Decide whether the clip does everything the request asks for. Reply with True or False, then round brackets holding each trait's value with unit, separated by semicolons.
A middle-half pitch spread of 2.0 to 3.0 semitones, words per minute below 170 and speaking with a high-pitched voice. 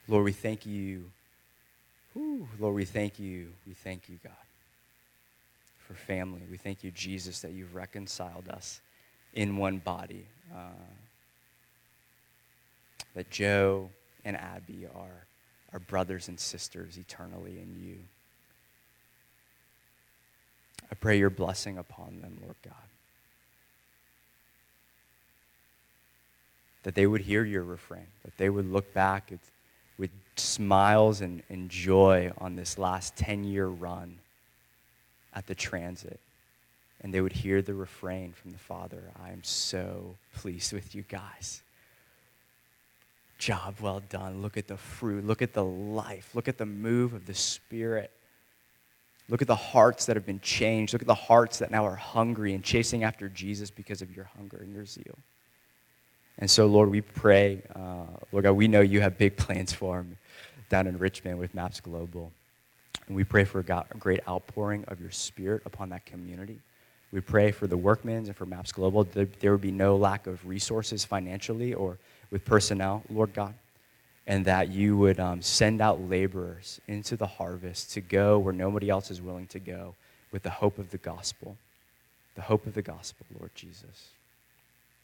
False (2.5 semitones; 160 wpm; 95 Hz)